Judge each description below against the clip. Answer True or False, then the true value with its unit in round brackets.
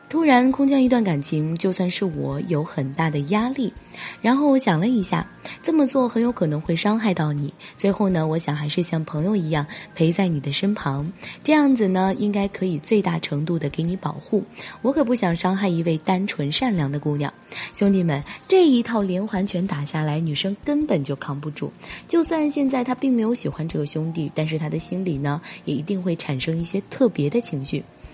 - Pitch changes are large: True (6.2 semitones)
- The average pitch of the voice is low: False (185 Hz)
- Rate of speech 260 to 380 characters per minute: True (300 characters per minute)